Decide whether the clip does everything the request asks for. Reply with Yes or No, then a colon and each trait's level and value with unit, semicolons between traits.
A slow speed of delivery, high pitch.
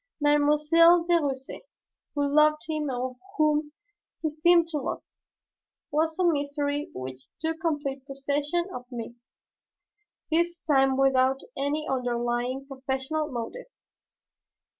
Yes: slow, 115 wpm; very high, 290 Hz